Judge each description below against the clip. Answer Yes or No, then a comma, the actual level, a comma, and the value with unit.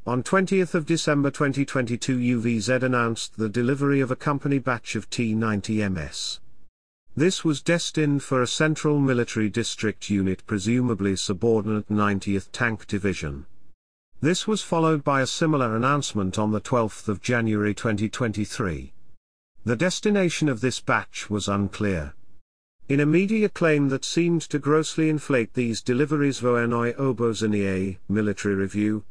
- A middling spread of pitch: No, wide, 5.8 semitones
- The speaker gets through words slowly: Yes, slow, 130 wpm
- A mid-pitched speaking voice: No, low, 120 Hz